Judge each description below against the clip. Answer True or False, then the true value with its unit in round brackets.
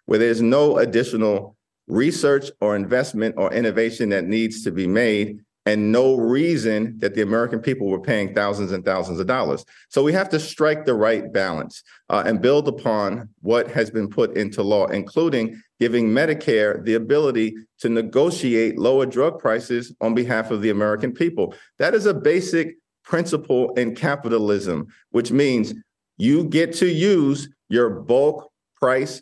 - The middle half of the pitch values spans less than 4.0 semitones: False (4.3 semitones)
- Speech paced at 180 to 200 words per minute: False (160 wpm)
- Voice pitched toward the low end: True (115 Hz)